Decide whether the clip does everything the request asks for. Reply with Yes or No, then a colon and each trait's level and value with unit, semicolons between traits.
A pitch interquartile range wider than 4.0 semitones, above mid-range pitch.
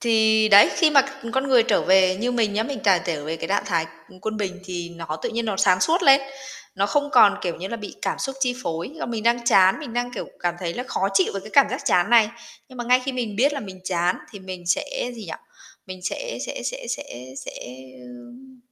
Yes: average, 5.1 semitones; high, 215 Hz